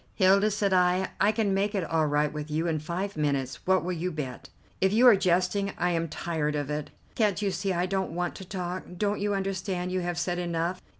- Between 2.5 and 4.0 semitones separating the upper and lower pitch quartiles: Yes, average, 3.0 semitones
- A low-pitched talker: No, medium, 180 Hz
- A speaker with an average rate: No, fast, 230 wpm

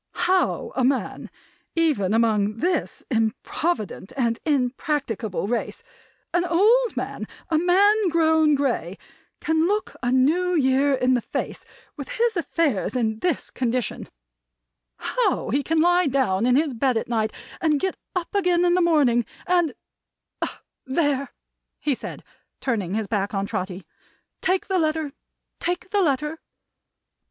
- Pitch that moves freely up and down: Yes, wide, 6.7 semitones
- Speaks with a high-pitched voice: Yes, very high, 285 Hz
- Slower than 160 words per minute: Yes, average, 140 wpm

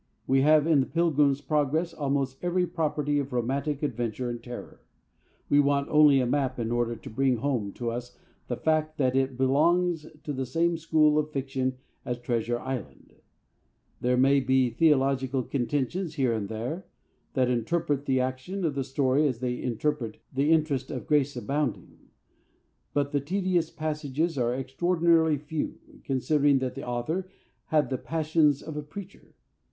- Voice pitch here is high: No, medium, 140 Hz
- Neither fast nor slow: Yes, average, 160 wpm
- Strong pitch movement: No, average, 3.2 semitones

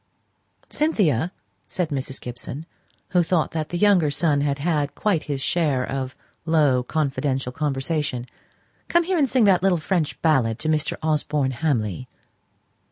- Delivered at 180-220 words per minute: No, average, 145 wpm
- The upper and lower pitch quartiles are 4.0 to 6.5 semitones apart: Yes, average, 4.4 semitones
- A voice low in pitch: No, medium, 150 Hz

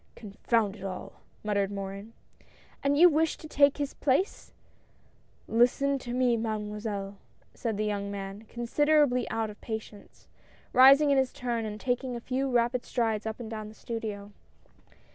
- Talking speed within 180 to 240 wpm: No, average, 170 wpm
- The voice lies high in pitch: Yes, high, 230 Hz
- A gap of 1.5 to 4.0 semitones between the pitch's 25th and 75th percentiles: Yes, average, 3.7 semitones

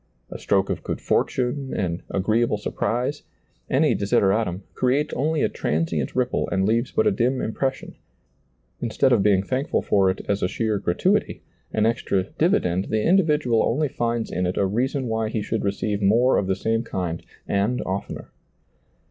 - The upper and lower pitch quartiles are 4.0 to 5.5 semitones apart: Yes, average, 4.7 semitones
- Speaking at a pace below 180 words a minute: Yes, average, 170 wpm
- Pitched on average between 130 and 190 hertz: No, low, 110 Hz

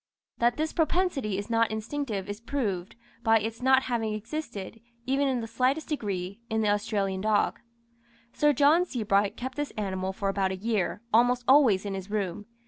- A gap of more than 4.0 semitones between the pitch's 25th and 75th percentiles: Yes, average, 4.6 semitones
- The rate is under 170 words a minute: No, average, 175 wpm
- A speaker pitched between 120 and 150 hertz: No, high, 225 Hz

